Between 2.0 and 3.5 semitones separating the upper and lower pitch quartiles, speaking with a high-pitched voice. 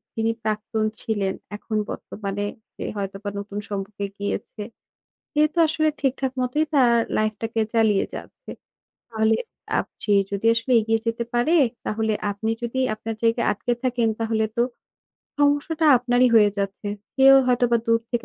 Yes: average, 2.7 semitones; high, 225 Hz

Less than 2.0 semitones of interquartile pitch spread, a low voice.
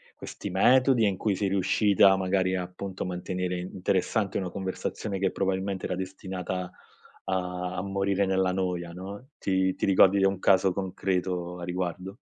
Yes: narrow, 1.2 semitones; very low, 95 Hz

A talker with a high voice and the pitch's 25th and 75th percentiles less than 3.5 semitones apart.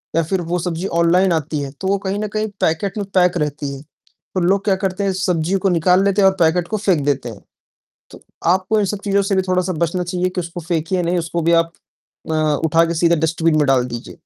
No: medium, 175 Hz; average, 2.7 semitones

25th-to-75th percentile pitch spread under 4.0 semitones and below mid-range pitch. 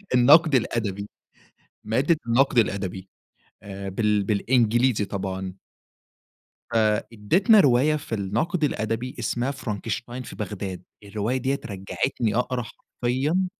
No: average, 4.3 semitones; low, 115 Hz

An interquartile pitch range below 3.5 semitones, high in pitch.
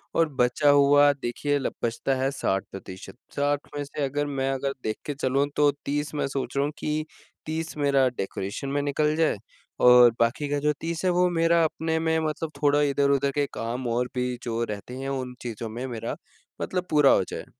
No: average, 3.0 semitones; medium, 140 Hz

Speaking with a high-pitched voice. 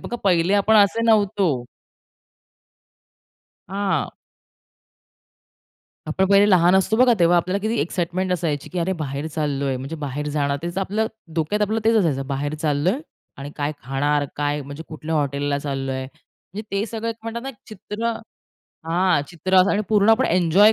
No: medium, 175 Hz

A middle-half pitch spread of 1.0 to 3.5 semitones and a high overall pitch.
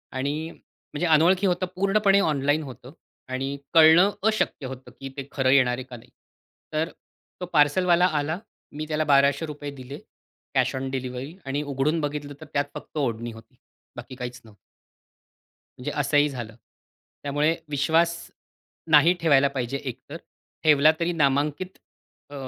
No: average, 3.2 semitones; medium, 145 Hz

